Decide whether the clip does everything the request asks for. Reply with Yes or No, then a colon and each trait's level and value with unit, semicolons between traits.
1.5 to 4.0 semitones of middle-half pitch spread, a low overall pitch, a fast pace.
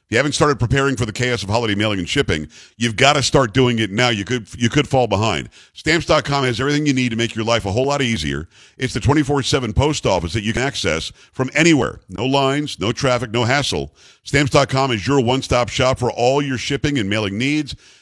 Yes: average, 3.6 semitones; low, 125 Hz; fast, 225 wpm